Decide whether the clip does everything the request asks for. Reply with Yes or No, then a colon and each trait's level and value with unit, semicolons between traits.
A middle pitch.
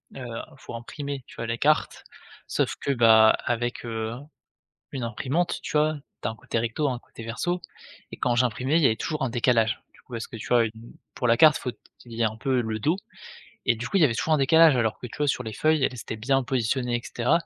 No: low, 120 Hz